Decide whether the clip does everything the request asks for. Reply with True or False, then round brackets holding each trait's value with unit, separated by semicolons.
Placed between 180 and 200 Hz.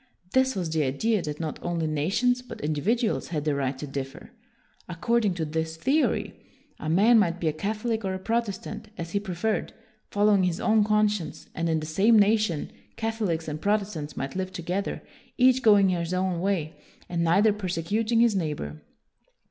True (185 Hz)